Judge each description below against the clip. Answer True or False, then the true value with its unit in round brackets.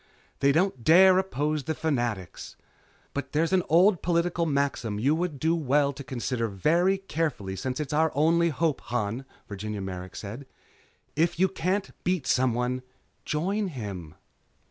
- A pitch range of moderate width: False (5.7 semitones)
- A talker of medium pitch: True (145 Hz)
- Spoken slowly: False (145 wpm)